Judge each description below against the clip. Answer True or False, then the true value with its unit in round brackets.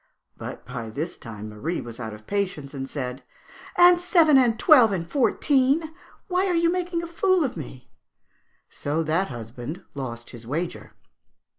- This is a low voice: False (170 Hz)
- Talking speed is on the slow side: False (165 wpm)